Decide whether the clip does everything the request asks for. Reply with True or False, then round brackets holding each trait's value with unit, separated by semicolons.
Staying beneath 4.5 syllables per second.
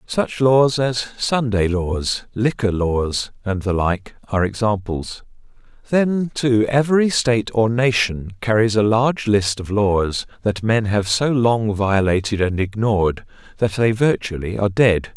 True (4.1 syllables/s)